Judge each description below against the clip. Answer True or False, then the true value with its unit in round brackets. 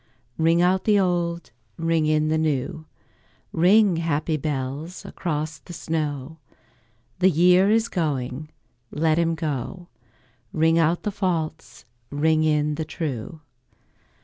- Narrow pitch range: True (2.3 semitones)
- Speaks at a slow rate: True (120 wpm)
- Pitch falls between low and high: True (160 Hz)